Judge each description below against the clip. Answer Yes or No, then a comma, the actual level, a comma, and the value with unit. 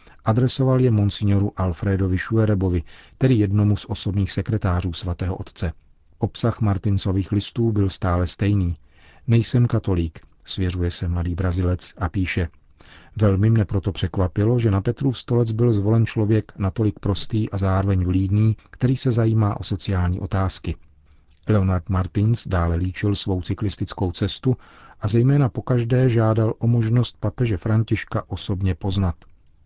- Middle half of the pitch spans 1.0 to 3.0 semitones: No, average, 3.4 semitones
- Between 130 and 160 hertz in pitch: No, low, 100 Hz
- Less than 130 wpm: No, average, 135 wpm